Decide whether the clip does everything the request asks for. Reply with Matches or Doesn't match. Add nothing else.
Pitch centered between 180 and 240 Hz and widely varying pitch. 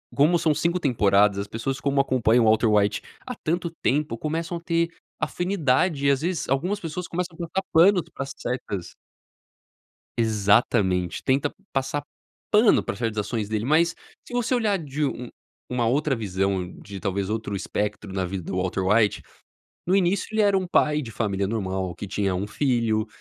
Doesn't match